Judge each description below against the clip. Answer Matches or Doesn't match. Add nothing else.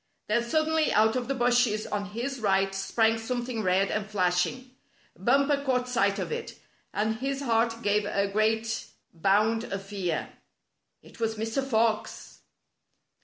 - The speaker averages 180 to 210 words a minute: Doesn't match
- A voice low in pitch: Doesn't match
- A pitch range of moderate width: Matches